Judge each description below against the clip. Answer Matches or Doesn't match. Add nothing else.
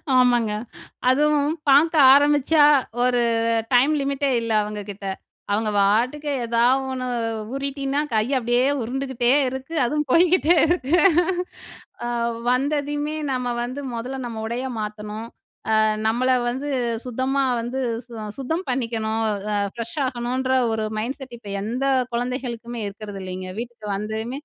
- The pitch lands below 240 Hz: Doesn't match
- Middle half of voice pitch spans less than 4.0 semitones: Matches